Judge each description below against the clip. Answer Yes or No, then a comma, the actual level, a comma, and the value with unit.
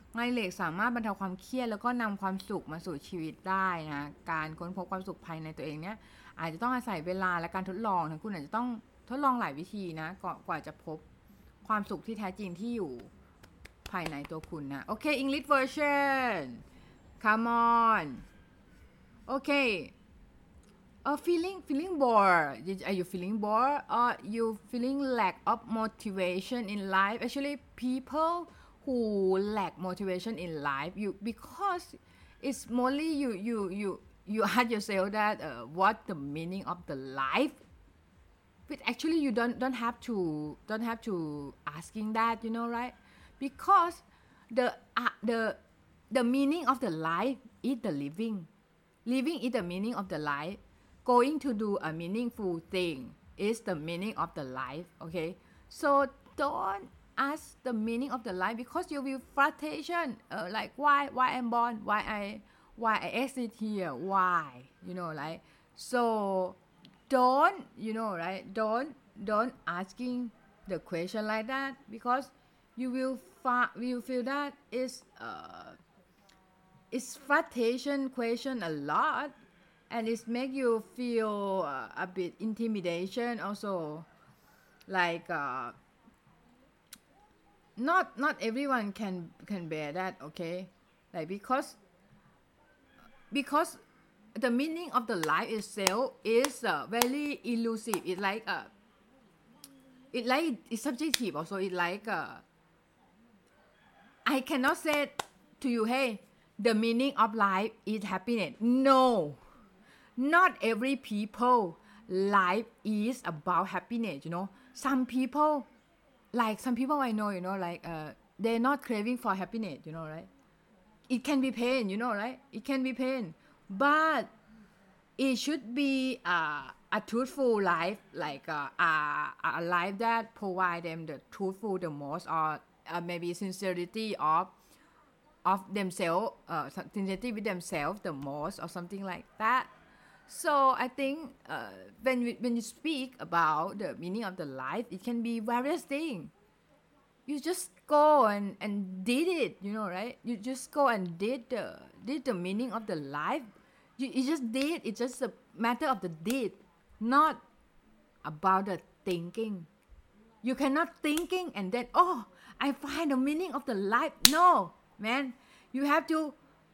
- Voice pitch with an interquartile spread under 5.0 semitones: No, wide, 5.5 semitones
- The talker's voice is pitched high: Yes, high, 225 Hz